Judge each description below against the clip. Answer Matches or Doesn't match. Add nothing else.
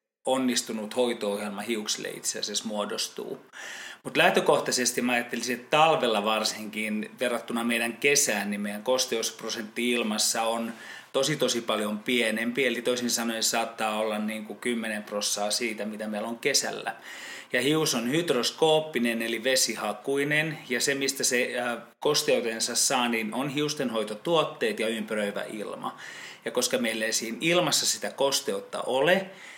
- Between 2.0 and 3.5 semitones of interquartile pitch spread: Matches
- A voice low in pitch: Matches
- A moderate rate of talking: Matches